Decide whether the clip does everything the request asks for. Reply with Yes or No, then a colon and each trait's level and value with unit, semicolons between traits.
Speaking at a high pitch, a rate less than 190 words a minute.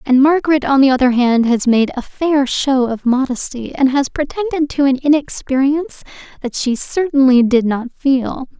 Yes: very high, 270 Hz; average, 175 wpm